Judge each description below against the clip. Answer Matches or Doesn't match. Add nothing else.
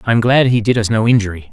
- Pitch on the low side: Matches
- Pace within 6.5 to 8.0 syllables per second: Matches